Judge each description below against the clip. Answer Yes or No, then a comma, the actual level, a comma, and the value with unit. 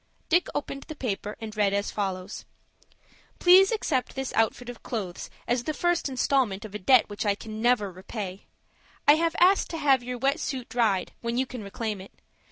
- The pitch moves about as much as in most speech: Yes, average, 5.0 semitones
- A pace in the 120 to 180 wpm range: No, average, 190 wpm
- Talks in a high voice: Yes, high, 240 Hz